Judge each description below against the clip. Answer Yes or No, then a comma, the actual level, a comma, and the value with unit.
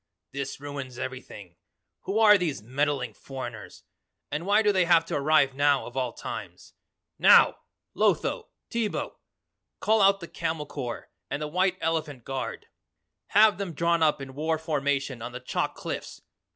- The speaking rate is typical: Yes, average, 155 wpm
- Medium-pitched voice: Yes, medium, 150 Hz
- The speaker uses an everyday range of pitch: Yes, average, 4.8 semitones